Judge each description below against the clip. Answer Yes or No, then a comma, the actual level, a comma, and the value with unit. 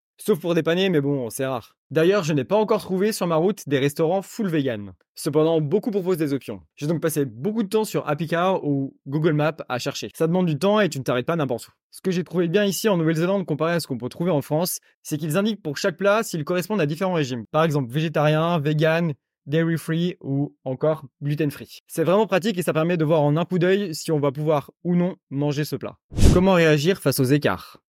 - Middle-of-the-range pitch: Yes, medium, 160 Hz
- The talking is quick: Yes, fast, 245 wpm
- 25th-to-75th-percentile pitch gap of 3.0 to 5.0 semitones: Yes, average, 4.1 semitones